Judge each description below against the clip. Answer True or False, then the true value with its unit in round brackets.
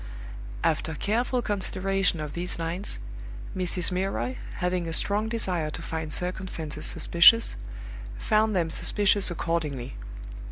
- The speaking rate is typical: False (115 wpm)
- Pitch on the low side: False (180 Hz)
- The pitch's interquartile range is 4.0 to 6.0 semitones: False (3.6 semitones)